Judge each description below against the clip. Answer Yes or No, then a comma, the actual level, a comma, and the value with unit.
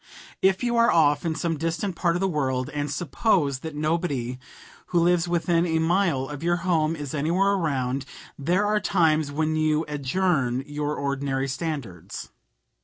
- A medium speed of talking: Yes, average, 165 wpm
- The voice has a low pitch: No, medium, 155 Hz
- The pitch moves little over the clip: No, average, 3.6 semitones